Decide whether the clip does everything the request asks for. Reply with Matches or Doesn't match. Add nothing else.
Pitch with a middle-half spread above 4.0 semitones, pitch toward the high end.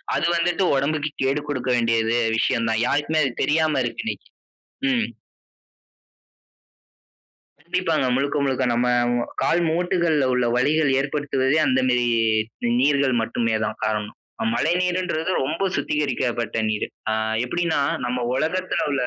Doesn't match